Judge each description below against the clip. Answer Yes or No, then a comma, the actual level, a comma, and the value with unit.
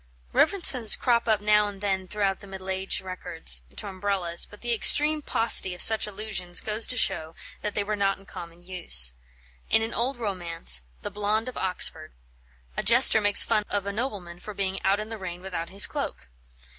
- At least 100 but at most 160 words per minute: No, average, 195 wpm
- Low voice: No, high, 200 Hz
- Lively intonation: No, average, 2.9 semitones